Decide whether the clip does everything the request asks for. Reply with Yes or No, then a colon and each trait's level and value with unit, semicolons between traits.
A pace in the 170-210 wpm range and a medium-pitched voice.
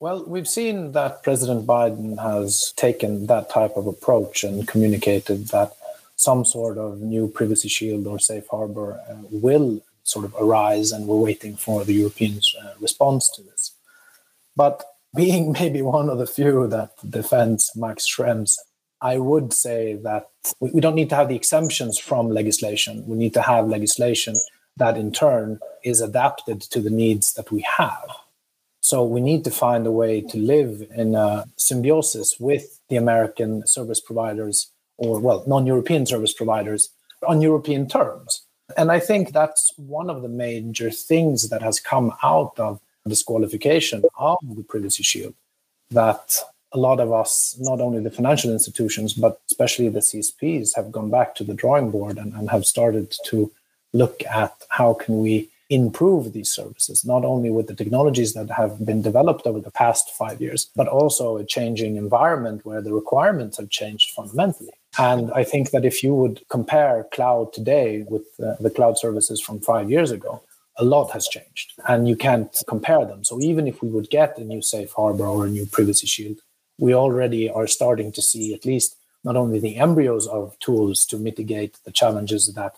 No: average, 180 wpm; low, 115 Hz